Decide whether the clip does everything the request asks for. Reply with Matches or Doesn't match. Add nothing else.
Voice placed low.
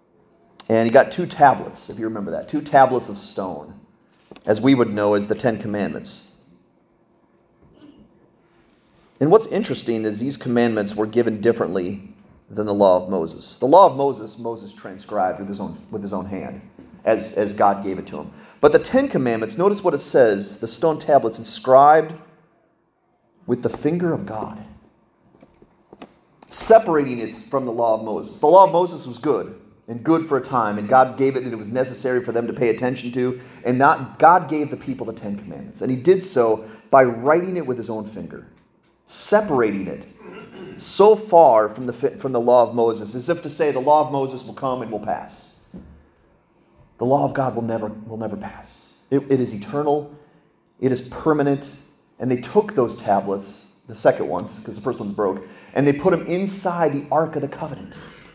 Matches